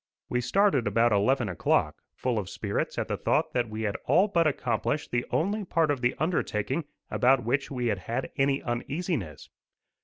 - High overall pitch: No, low, 130 Hz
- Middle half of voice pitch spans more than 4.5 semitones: Yes, average, 5.0 semitones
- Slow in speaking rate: No, average, 180 wpm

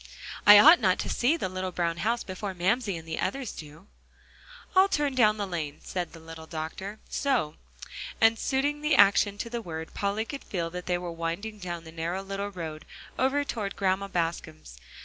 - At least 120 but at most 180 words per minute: No, average, 190 wpm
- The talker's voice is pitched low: No, high, 190 Hz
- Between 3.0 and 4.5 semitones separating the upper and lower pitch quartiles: No, average, 5.0 semitones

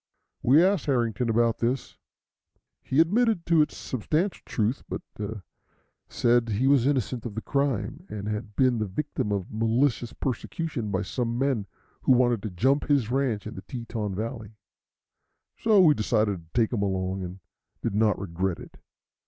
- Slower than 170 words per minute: Yes, average, 160 wpm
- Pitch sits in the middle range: No, low, 120 Hz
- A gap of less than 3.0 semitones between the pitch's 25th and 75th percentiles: No, average, 4.6 semitones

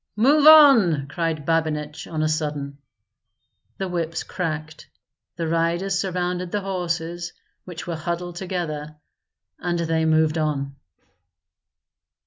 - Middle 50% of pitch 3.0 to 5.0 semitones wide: No, narrow, 2.4 semitones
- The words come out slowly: Yes, slow, 115 wpm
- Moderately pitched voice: Yes, medium, 165 Hz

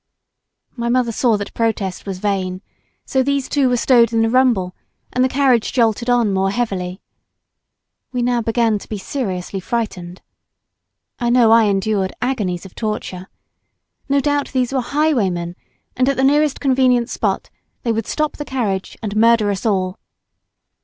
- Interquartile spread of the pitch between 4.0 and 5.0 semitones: Yes, average, 4.5 semitones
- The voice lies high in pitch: Yes, high, 230 Hz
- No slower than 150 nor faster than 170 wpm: Yes, average, 160 wpm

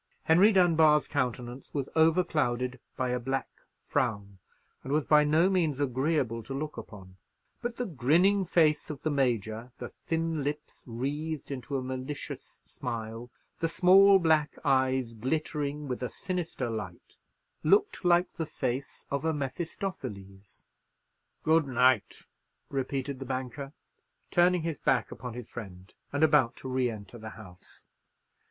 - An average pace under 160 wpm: Yes, average, 140 wpm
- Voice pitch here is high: No, low, 135 Hz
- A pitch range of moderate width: Yes, average, 4.6 semitones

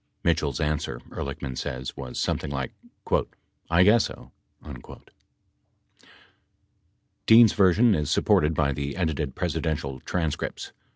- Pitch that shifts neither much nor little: Yes, average, 4.3 semitones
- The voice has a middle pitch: No, very low, 75 Hz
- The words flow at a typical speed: No, slow, 115 wpm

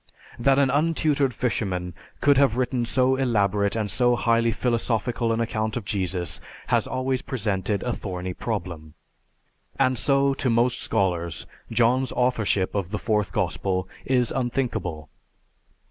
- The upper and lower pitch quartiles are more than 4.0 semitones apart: Yes, average, 4.5 semitones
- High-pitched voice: No, low, 115 Hz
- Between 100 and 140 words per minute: Yes, slow, 135 wpm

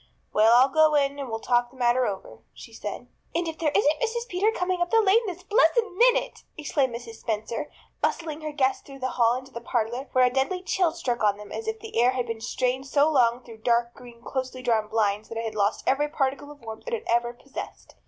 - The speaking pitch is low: No, very high, 260 Hz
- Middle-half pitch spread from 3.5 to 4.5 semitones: No, average, 5.2 semitones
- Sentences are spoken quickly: Yes, fast, 235 wpm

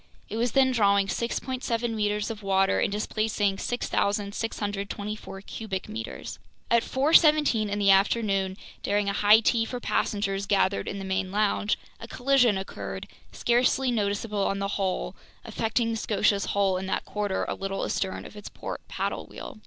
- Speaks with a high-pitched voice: Yes, high, 205 Hz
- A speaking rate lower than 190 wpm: Yes, average, 160 wpm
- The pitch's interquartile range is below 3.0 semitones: Yes, narrow, 2.5 semitones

